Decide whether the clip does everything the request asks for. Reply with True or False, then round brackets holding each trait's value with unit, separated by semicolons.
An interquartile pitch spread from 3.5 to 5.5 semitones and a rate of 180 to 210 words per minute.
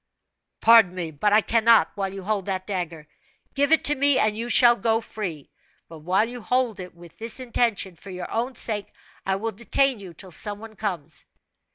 True (4.2 semitones; 200 wpm)